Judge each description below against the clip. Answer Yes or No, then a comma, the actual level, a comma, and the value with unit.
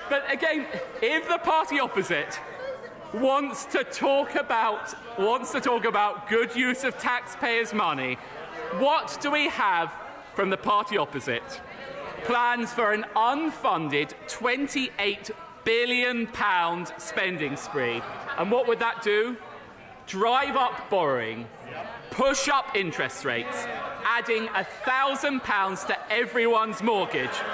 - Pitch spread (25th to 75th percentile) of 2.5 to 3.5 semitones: No, average, 4.7 semitones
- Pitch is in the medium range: No, high, 240 Hz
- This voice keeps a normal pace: No, slow, 115 wpm